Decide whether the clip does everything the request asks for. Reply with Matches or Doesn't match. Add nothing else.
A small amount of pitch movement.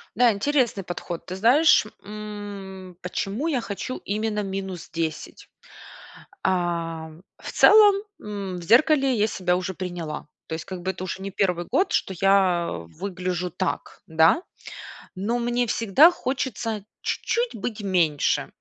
Doesn't match